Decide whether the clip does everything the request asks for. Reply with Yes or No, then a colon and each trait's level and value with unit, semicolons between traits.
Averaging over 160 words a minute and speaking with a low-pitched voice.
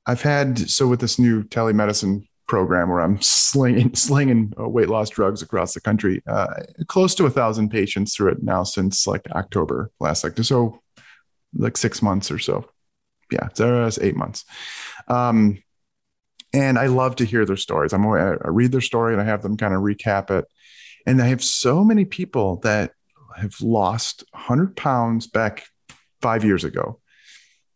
Yes: average, 170 wpm; low, 115 Hz